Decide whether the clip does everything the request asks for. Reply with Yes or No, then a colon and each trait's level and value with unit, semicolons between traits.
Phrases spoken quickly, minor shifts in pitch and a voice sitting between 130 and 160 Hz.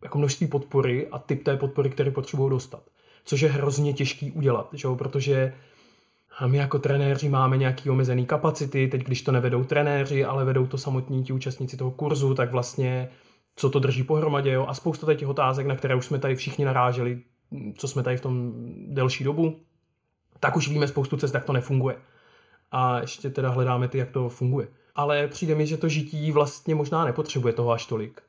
Yes: fast, 195 wpm; narrow, 2.1 semitones; medium, 140 Hz